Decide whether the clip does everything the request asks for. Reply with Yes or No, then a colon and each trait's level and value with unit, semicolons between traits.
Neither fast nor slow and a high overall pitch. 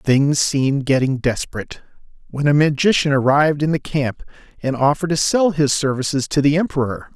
No: average, 170 wpm; medium, 140 Hz